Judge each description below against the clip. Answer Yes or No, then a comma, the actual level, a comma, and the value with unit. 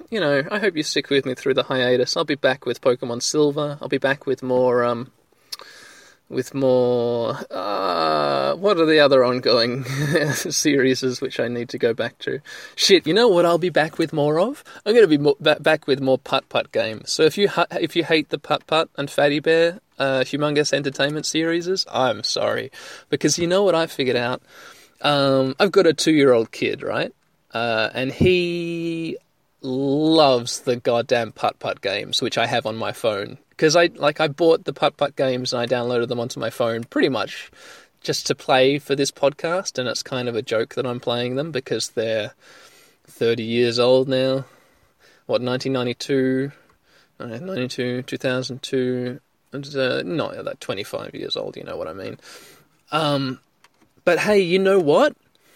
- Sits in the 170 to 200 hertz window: No, medium, 140 Hz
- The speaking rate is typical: Yes, average, 185 wpm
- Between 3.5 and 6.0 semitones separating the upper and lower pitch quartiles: Yes, average, 4.2 semitones